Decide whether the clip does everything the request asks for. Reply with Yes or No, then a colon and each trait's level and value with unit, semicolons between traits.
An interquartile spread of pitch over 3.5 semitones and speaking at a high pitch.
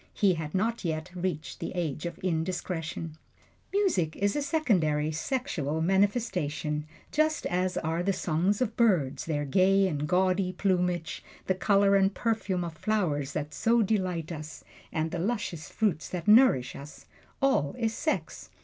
No: average, 4.5 semitones; medium, 180 Hz